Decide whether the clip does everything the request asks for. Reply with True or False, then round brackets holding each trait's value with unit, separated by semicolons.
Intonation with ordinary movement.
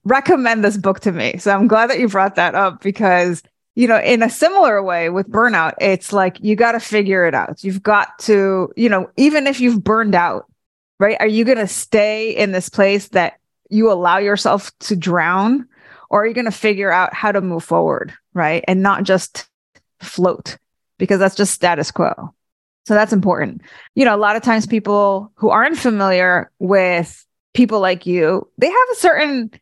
True (3.4 semitones)